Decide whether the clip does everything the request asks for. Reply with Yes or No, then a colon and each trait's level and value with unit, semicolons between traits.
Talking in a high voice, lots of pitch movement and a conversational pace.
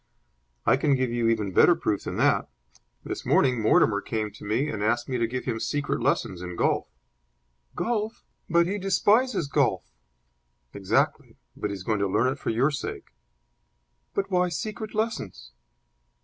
No: low, 125 Hz; wide, 8.4 semitones; average, 165 wpm